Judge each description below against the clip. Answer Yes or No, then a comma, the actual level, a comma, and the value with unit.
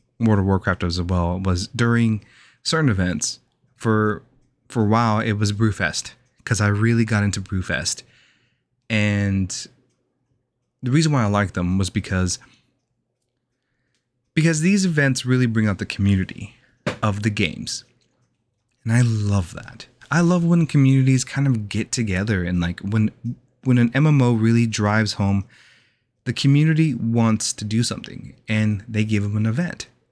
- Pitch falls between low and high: No, low, 115 Hz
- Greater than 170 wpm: No, average, 150 wpm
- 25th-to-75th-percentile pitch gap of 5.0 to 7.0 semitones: No, average, 3.6 semitones